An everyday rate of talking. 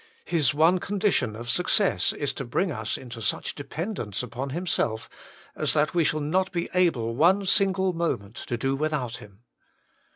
Yes: average, 165 wpm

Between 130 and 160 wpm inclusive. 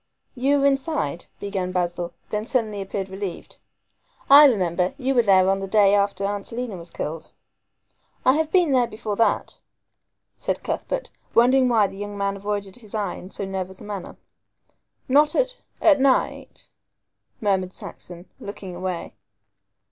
Yes: average, 155 wpm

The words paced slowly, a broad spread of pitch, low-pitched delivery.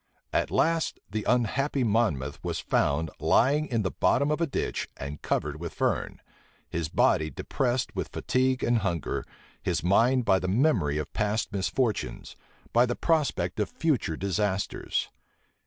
No: average, 150 wpm; wide, 7.2 semitones; low, 110 Hz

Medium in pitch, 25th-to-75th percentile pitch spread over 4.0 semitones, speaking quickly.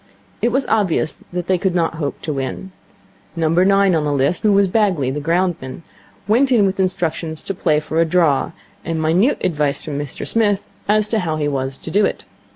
Yes: medium, 175 Hz; average, 4.6 semitones; fast, 210 wpm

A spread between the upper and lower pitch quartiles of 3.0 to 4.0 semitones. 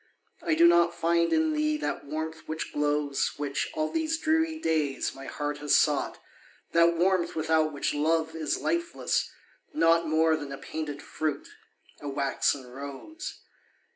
No: narrow, 2.6 semitones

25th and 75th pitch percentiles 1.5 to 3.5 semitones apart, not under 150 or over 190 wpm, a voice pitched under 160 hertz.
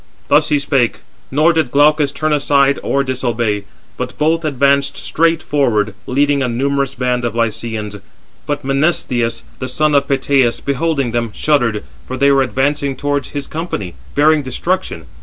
Yes: average, 3.2 semitones; average, 155 wpm; medium, 140 Hz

